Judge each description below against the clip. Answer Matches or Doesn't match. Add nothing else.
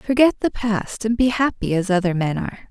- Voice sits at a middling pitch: Doesn't match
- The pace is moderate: Doesn't match